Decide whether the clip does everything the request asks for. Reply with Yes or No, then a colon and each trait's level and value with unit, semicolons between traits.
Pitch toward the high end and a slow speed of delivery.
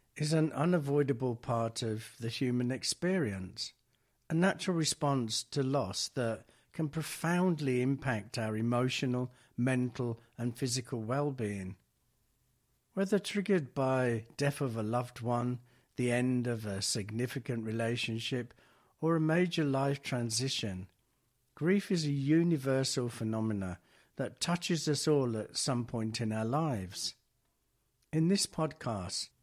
No: low, 125 Hz; slow, 120 wpm